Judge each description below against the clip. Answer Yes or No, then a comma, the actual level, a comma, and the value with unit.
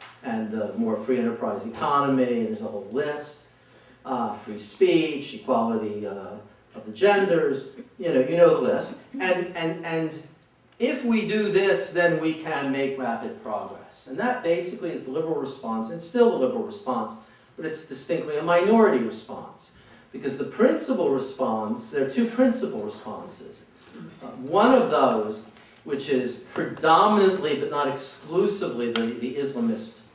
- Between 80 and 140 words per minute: No, average, 155 wpm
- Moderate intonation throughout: No, wide, 7.2 semitones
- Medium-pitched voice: Yes, medium, 160 Hz